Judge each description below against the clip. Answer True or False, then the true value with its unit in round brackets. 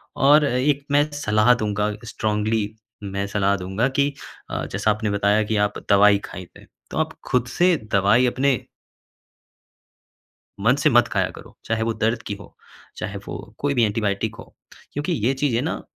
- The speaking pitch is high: False (110 Hz)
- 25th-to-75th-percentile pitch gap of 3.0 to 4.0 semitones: False (4.4 semitones)